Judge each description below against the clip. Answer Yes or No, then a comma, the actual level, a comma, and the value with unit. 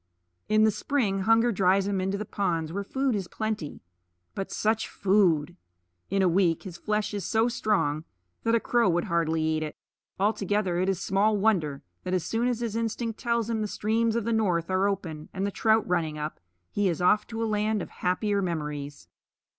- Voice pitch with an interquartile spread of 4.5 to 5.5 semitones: No, average, 3.9 semitones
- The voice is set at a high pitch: Yes, high, 200 Hz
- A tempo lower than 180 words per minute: No, average, 200 wpm